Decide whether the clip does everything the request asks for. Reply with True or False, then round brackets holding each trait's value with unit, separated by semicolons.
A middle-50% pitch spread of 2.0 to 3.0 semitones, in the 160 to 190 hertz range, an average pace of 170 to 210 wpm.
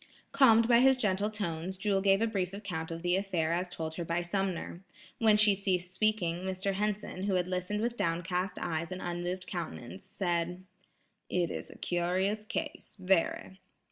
True (2.7 semitones; 185 Hz; 175 wpm)